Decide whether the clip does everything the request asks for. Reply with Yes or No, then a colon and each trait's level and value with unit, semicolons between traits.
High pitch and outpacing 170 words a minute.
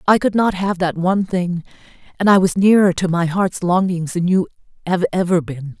No: medium, 180 Hz; fast, 205 wpm